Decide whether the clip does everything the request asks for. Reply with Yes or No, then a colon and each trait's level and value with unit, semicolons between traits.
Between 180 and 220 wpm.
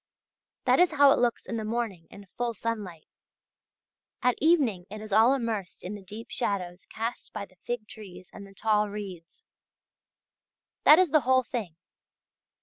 No: average, 165 wpm